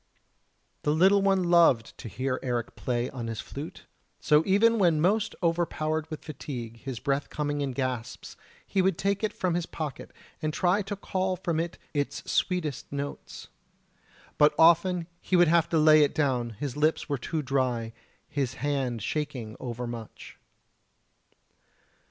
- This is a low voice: No, medium, 150 Hz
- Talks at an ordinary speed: Yes, average, 155 wpm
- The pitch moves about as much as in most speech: Yes, average, 5.0 semitones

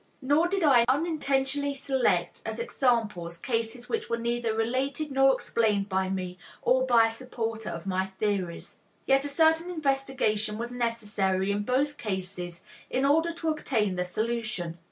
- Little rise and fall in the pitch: No, average, 4.9 semitones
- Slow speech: No, average, 155 wpm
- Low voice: No, high, 235 Hz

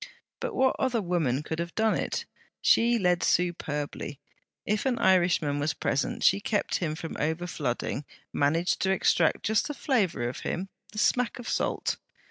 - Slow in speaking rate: No, average, 160 wpm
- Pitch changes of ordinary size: No, wide, 6.1 semitones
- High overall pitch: No, medium, 175 Hz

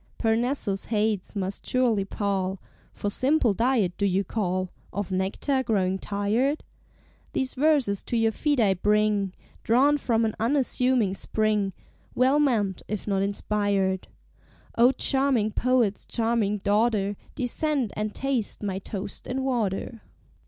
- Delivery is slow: Yes, slow, 130 wpm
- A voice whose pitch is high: Yes, high, 215 Hz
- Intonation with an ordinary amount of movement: Yes, average, 4.2 semitones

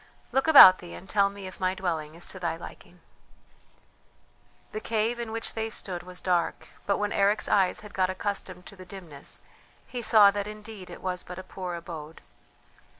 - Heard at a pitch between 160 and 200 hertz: Yes, high, 190 Hz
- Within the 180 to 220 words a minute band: Yes, average, 190 wpm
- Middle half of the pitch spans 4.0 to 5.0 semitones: No, average, 2.7 semitones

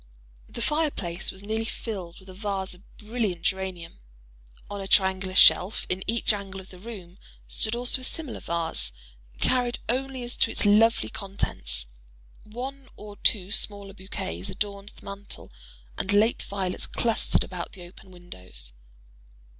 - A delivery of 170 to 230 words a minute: No, average, 155 wpm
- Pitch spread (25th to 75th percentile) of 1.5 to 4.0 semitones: Yes, average, 3.5 semitones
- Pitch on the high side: Yes, high, 200 Hz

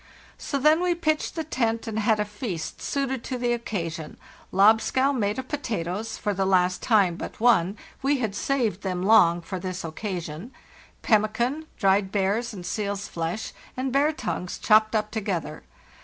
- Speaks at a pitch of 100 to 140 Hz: No, high, 215 Hz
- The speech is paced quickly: No, average, 165 wpm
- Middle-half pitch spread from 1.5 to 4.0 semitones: No, average, 5.0 semitones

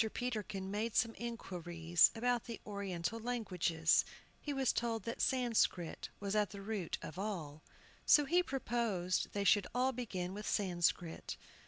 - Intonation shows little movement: No, average, 4.7 semitones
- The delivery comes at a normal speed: Yes, average, 145 wpm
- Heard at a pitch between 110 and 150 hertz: No, high, 210 Hz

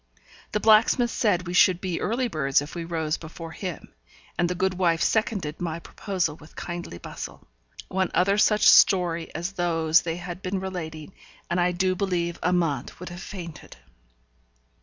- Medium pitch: Yes, medium, 175 Hz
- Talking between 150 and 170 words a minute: Yes, average, 165 wpm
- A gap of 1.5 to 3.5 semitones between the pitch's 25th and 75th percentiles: Yes, narrow, 2.4 semitones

